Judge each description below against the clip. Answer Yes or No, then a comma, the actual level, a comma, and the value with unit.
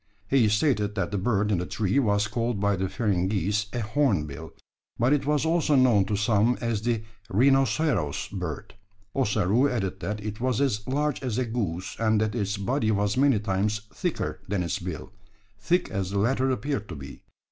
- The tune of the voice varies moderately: Yes, average, 4.3 semitones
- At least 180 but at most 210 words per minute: Yes, average, 185 wpm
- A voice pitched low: Yes, low, 105 Hz